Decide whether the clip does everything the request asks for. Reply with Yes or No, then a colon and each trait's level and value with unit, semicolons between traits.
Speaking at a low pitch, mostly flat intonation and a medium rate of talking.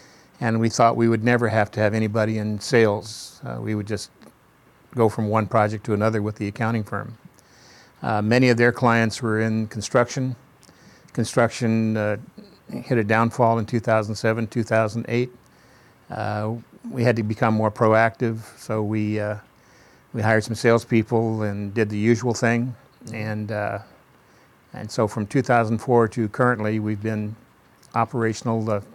Yes: low, 110 Hz; narrow, 1.6 semitones; average, 150 wpm